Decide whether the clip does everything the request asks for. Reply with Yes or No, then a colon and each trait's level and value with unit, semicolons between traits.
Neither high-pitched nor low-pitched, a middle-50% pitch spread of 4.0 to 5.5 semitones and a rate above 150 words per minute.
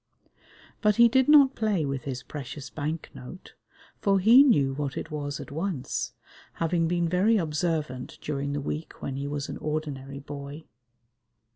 Yes: medium, 155 Hz; average, 4.7 semitones; average, 160 wpm